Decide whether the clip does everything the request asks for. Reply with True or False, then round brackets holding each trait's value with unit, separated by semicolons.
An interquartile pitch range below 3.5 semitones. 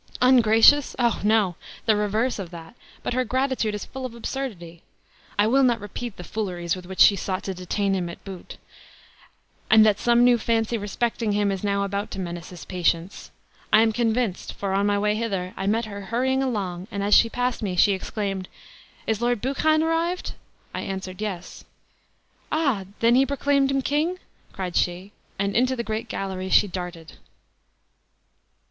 False (4.1 semitones)